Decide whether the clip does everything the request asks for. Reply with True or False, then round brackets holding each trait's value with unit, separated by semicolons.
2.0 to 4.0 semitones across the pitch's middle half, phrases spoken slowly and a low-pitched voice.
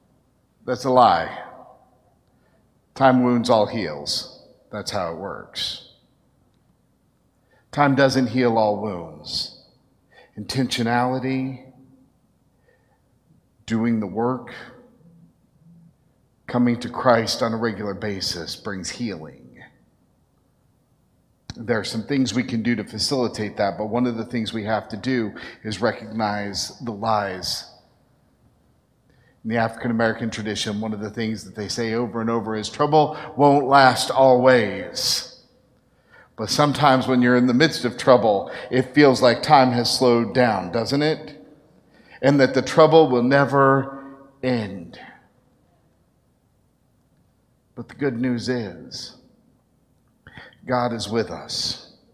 True (2.9 semitones; 120 wpm; 125 Hz)